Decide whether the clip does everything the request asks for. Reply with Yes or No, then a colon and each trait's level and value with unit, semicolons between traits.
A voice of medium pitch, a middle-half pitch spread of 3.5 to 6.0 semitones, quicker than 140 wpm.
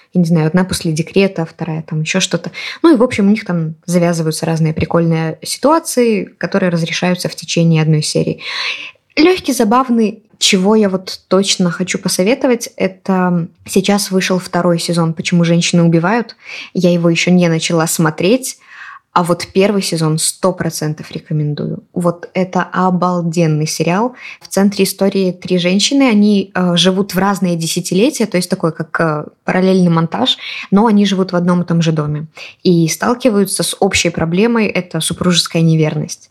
No: medium, 180 Hz; average, 3.0 semitones; average, 155 wpm